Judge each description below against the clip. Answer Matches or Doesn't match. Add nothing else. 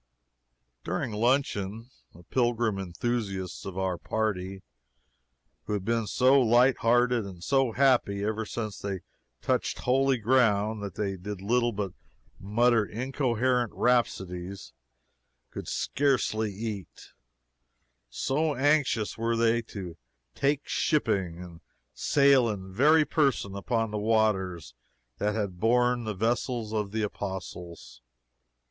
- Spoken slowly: Matches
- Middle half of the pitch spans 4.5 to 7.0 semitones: Doesn't match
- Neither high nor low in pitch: Doesn't match